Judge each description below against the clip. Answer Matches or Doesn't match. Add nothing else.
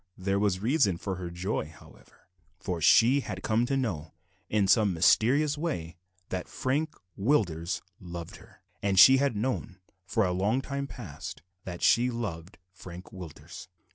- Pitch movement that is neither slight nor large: Doesn't match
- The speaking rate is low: Doesn't match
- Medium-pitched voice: Doesn't match